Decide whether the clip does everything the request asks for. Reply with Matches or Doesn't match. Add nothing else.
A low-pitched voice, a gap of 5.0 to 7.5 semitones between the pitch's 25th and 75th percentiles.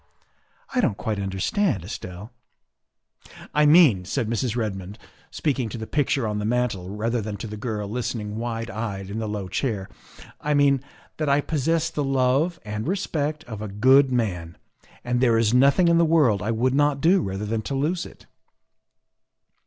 Matches